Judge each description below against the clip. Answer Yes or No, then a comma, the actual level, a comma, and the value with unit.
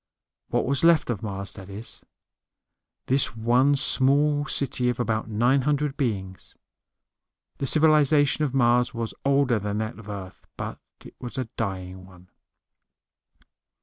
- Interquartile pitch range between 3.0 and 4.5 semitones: No, average, 5.0 semitones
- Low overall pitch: Yes, low, 120 Hz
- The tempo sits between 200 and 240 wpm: No, average, 140 wpm